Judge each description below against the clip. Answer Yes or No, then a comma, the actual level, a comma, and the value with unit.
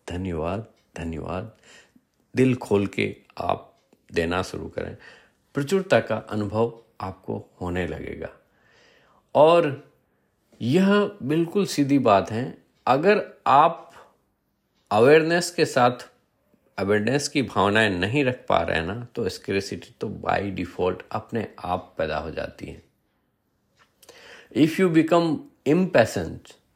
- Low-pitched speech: Yes, low, 110 Hz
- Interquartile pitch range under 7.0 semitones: No, wide, 7.4 semitones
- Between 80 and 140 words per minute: Yes, slow, 110 wpm